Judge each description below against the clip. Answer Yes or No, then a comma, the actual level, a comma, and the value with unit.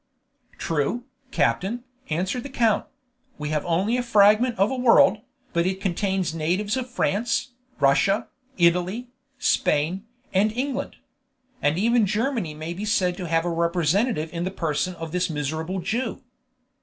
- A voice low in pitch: No, high, 190 Hz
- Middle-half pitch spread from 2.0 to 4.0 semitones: No, wide, 5.4 semitones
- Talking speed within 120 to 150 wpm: Yes, average, 145 wpm